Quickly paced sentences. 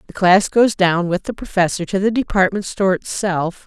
No: average, 195 wpm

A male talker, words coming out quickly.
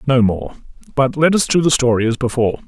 Yes: male; fast, 225 wpm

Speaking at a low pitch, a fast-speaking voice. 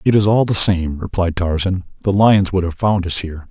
Yes: very low, 95 Hz; fast, 240 wpm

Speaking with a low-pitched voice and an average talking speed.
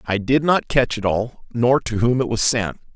No: low, 120 Hz; fast, 245 wpm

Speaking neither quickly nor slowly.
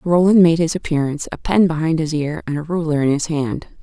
No: fast, 235 wpm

